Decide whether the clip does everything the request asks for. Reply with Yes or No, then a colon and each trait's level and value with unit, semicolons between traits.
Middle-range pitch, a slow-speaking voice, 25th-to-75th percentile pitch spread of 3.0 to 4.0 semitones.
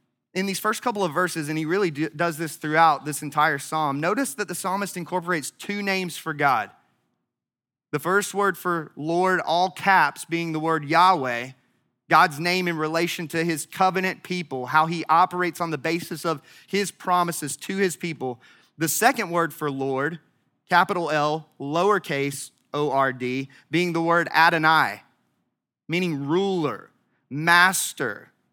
No: medium, 165 Hz; average, 155 wpm; average, 3.3 semitones